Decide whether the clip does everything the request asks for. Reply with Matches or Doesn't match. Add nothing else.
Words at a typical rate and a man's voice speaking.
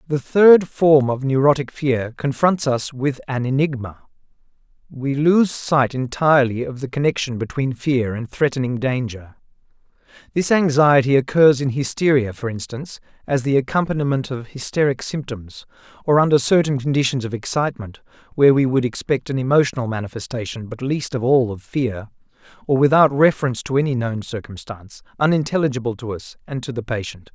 Matches